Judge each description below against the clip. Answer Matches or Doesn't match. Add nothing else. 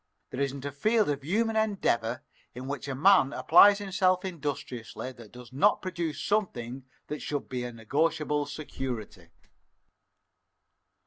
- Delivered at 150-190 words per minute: Doesn't match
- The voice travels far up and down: Matches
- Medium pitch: Matches